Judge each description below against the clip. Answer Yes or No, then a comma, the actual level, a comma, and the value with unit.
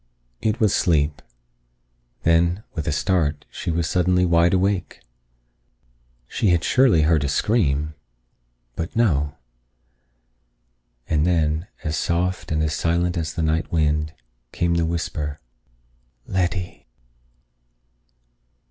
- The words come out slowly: Yes, slow, 110 wpm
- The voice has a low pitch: Yes, very low, 85 Hz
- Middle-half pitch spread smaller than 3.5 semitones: Yes, average, 2.8 semitones